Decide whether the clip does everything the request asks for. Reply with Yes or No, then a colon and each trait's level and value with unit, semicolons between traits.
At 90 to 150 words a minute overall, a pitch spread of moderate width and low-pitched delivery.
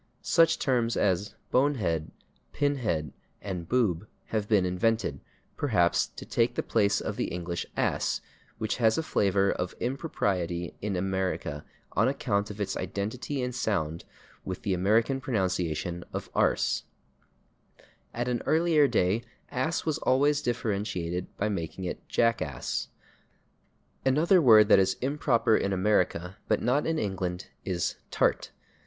No: slow, 135 wpm; wide, 5.7 semitones; low, 105 Hz